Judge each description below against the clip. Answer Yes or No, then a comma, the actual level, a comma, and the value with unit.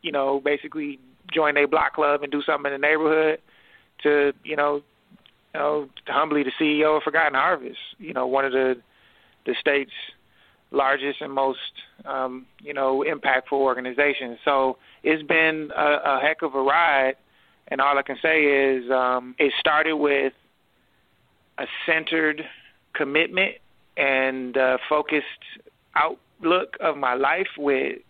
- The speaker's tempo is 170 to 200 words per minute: No, average, 145 wpm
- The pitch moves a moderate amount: No, narrow, 2.3 semitones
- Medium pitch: Yes, medium, 145 Hz